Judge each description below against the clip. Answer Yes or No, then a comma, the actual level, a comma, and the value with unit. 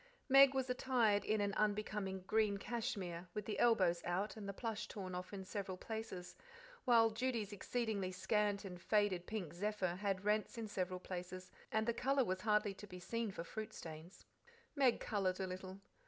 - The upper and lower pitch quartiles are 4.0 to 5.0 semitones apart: No, average, 3.0 semitones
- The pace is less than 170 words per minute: No, average, 180 wpm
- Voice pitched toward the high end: Yes, high, 205 Hz